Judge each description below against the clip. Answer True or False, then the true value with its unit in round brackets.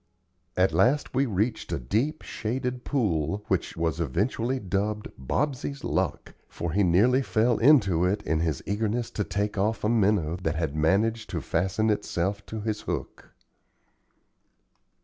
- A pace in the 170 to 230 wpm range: False (150 wpm)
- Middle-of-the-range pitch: False (105 Hz)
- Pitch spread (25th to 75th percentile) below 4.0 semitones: False (4.8 semitones)